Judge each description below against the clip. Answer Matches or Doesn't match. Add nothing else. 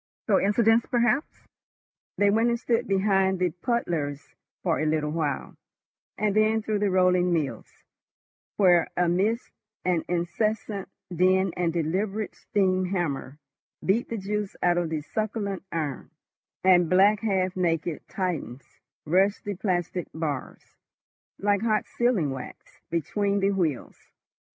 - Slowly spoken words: Matches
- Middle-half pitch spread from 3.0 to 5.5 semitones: Matches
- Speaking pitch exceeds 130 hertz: Matches